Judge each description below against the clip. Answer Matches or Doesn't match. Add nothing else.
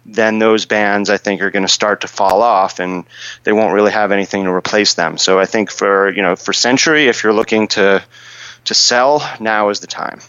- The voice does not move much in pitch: Matches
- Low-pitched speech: Matches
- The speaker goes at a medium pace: Doesn't match